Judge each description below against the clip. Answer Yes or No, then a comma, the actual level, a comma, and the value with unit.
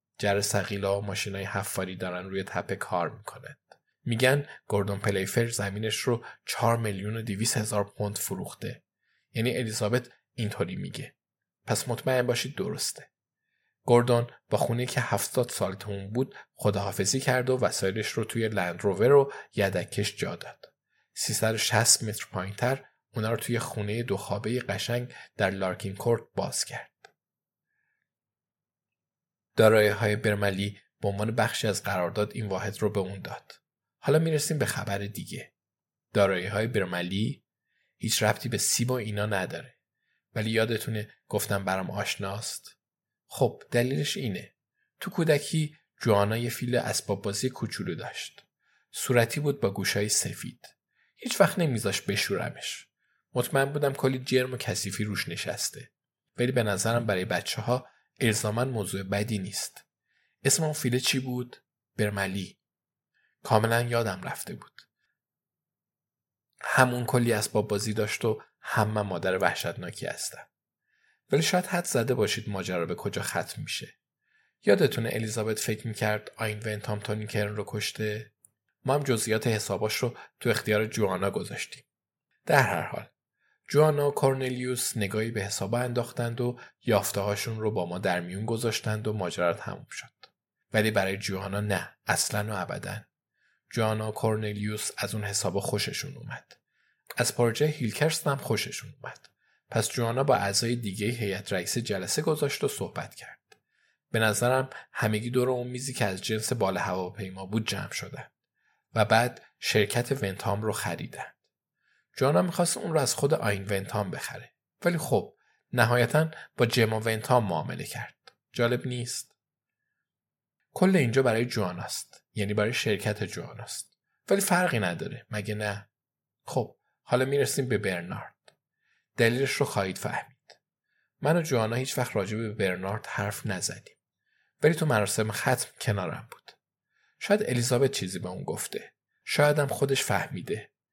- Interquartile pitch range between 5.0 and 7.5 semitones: No, average, 3.5 semitones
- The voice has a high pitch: No, low, 110 Hz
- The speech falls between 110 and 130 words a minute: No, average, 140 wpm